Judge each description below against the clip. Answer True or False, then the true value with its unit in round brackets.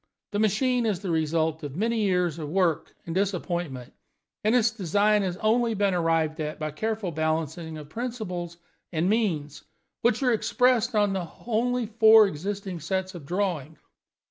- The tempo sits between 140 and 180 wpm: True (165 wpm)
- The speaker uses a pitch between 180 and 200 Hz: True (190 Hz)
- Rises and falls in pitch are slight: False (5.1 semitones)